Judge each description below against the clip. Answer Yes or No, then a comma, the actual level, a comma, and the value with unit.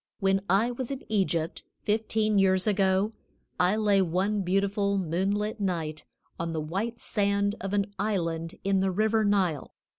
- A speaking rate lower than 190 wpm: Yes, average, 150 wpm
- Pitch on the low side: No, high, 195 Hz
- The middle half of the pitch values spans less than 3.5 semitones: Yes, narrow, 2.4 semitones